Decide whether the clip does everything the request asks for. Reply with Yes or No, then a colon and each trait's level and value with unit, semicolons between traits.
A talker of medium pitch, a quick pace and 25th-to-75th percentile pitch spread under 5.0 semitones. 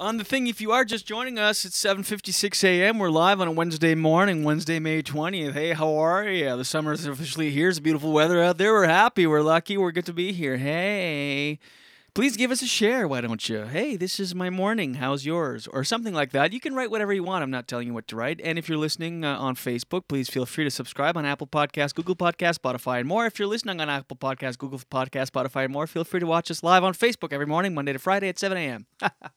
No: medium, 165 Hz; fast, 255 wpm; average, 5.3 semitones